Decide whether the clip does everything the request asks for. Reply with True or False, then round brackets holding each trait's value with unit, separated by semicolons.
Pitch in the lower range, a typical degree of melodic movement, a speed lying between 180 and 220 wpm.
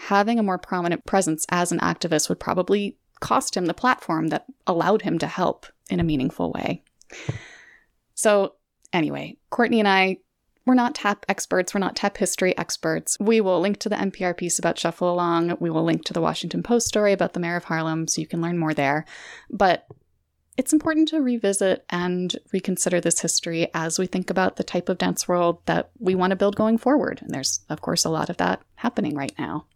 False (185 Hz; 3.3 semitones; 205 wpm)